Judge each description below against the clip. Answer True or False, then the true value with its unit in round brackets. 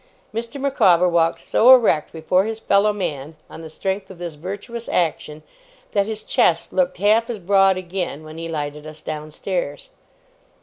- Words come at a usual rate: True (165 wpm)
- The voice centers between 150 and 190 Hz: True (185 Hz)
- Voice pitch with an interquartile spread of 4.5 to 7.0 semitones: True (4.9 semitones)